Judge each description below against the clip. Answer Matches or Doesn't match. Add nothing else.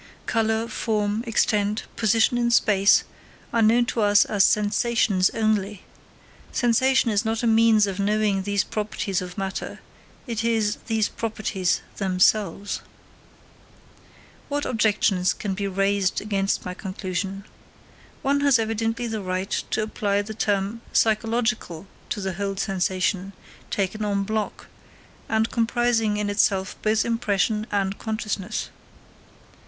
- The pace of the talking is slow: Matches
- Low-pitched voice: Doesn't match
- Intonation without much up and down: Matches